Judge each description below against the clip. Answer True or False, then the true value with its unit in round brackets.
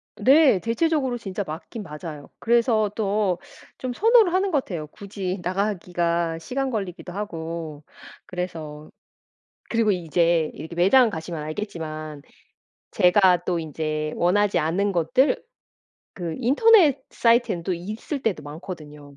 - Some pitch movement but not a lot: False (6.0 semitones)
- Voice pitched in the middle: True (180 Hz)